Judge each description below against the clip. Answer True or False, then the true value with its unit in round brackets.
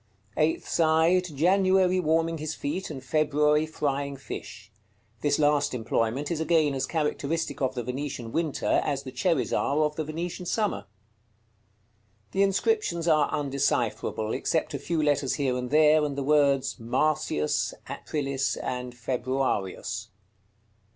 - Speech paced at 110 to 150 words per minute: True (135 wpm)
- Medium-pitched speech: True (150 Hz)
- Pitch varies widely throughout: False (3.3 semitones)